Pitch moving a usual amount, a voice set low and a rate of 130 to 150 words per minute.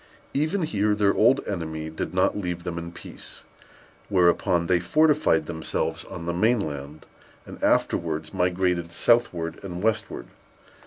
Yes: average, 4.1 semitones; very low, 90 Hz; average, 140 wpm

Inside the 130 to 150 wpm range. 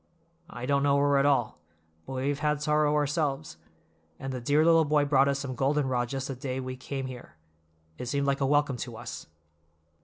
No: fast, 205 wpm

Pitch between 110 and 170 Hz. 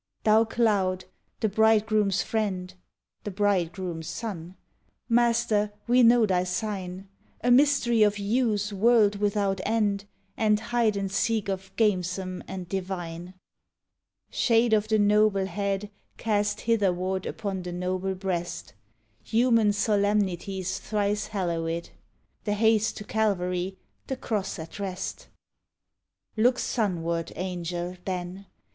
No: high, 200 Hz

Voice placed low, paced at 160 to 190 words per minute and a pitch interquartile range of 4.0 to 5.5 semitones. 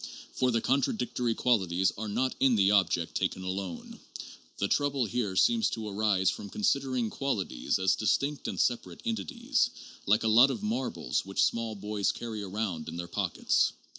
Yes: low, 110 Hz; average, 165 wpm; average, 4.6 semitones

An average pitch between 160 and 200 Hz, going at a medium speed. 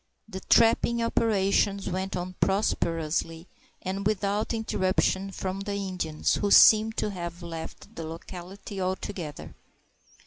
No: high, 190 Hz; slow, 115 wpm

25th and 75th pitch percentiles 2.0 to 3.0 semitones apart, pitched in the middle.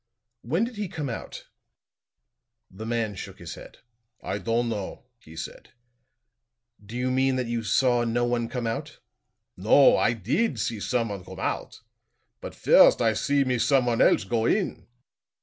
No: narrow, 2.6 semitones; low, 120 Hz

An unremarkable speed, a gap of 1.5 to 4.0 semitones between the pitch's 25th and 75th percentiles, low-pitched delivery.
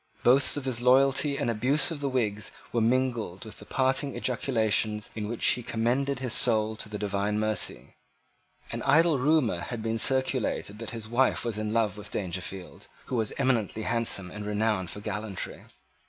Yes: average, 175 wpm; average, 3.6 semitones; low, 115 Hz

